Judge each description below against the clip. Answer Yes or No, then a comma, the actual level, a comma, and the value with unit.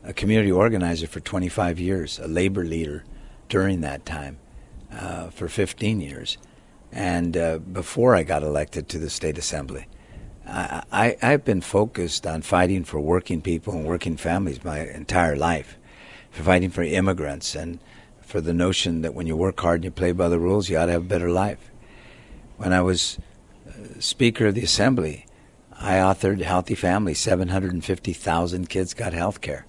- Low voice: Yes, very low, 90 Hz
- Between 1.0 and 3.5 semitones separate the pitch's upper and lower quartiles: Yes, narrow, 2.5 semitones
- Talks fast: No, average, 170 wpm